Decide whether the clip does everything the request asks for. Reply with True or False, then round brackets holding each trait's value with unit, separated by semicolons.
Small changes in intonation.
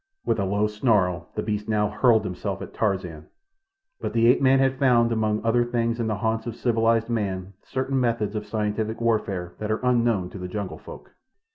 True (2.3 semitones)